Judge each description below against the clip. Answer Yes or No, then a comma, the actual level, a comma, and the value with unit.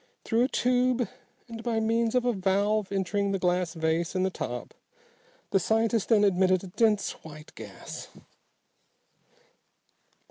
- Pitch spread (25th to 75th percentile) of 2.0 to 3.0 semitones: No, average, 3.6 semitones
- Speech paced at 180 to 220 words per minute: No, average, 140 wpm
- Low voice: No, high, 205 Hz